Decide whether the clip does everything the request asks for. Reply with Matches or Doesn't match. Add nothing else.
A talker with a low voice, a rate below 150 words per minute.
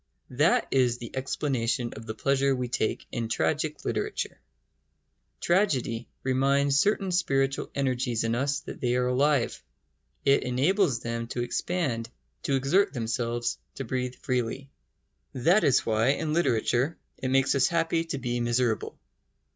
Matches